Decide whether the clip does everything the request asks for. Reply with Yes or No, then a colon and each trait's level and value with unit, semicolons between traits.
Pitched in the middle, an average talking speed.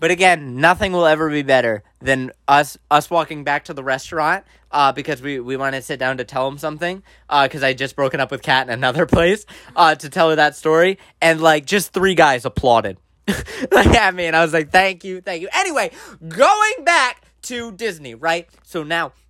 No: medium, 160 Hz; fast, 215 wpm